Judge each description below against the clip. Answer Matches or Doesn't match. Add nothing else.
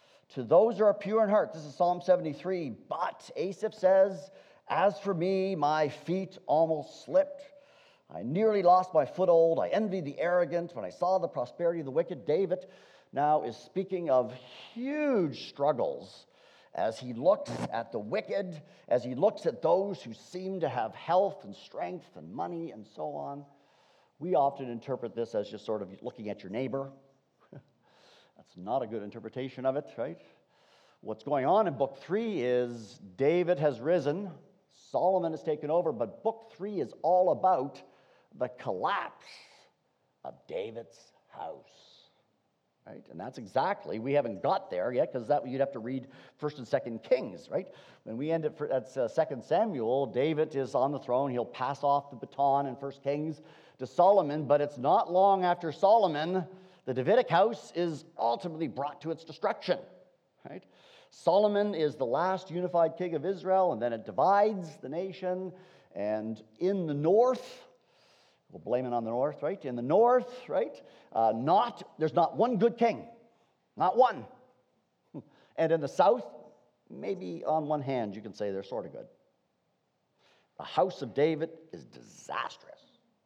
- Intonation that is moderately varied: Doesn't match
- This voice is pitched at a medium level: Matches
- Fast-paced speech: Doesn't match